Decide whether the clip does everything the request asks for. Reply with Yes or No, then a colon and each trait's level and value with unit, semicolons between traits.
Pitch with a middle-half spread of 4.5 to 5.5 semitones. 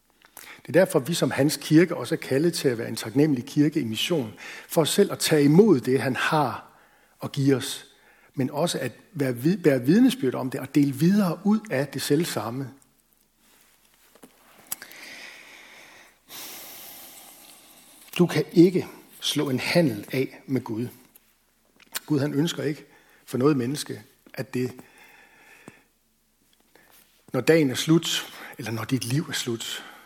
No: average, 3.8 semitones